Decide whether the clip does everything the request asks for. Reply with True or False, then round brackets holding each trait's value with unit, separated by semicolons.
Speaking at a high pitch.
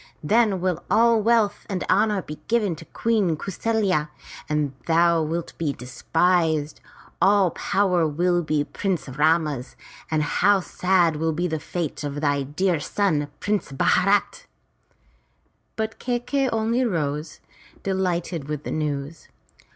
False (170 Hz)